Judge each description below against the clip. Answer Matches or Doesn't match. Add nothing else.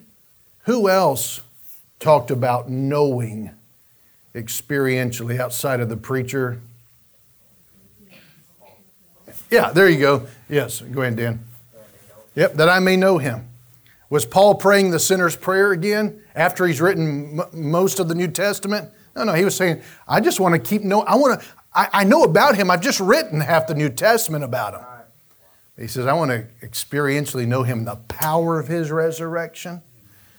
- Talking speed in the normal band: Matches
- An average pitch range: Doesn't match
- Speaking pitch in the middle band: Matches